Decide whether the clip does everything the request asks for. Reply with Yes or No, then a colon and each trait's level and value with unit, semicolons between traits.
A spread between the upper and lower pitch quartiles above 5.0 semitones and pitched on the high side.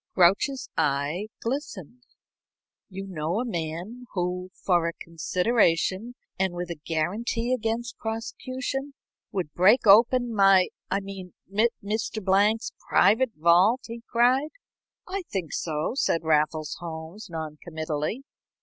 Yes: wide, 5.6 semitones; high, 195 Hz